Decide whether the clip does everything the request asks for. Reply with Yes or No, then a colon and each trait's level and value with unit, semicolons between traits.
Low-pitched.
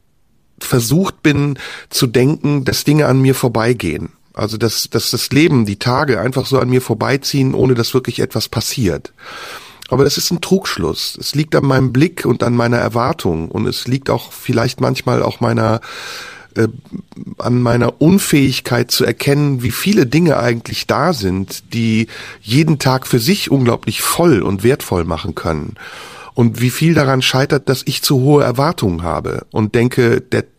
Yes: low, 130 Hz